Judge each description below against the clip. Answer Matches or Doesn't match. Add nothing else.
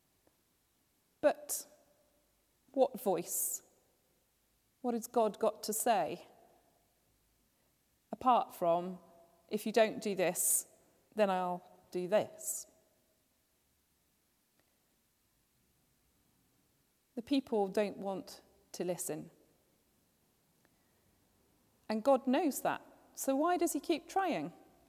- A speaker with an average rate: Doesn't match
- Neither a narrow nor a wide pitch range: Doesn't match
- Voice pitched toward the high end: Matches